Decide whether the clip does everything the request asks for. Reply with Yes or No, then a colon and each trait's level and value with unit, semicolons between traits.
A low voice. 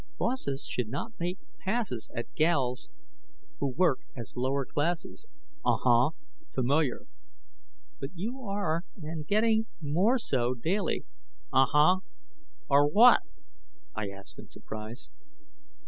No: medium, 150 Hz